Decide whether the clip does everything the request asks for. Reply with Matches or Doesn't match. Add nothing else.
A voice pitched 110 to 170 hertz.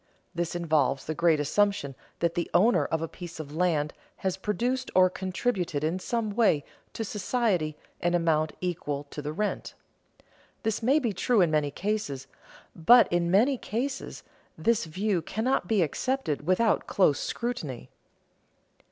Doesn't match